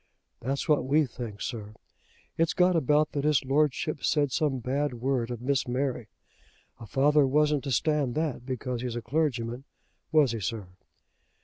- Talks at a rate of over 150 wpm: Yes, average, 165 wpm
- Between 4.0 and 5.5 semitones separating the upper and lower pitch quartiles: No, average, 3.5 semitones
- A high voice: No, low, 135 Hz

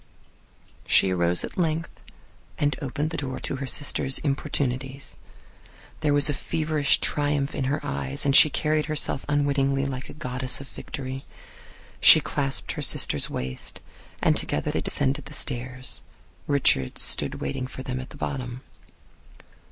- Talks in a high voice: No, low, 135 Hz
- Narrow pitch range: Yes, narrow, 2.2 semitones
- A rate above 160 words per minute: No, average, 150 wpm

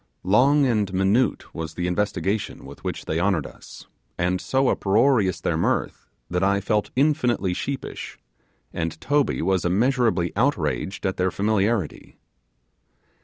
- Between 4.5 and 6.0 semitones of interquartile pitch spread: Yes, average, 5.3 semitones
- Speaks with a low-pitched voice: Yes, low, 100 Hz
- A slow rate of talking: Yes, slow, 130 wpm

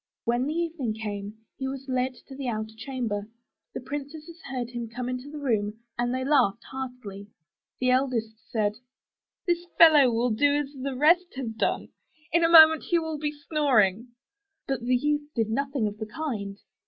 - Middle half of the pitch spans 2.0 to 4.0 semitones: No, average, 4.7 semitones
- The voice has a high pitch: Yes, very high, 255 Hz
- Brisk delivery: No, average, 180 wpm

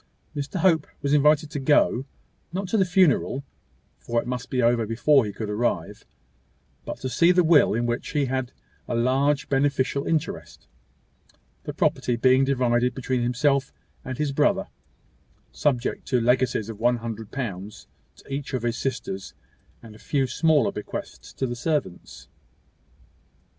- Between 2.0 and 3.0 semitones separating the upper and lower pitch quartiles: No, average, 3.4 semitones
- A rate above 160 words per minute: No, average, 155 wpm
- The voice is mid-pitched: No, low, 130 Hz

